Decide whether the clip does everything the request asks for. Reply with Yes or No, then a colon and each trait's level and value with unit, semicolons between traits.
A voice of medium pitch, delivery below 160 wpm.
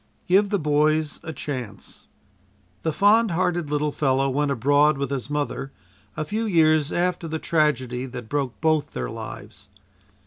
Yes: medium, 150 Hz; average, 150 wpm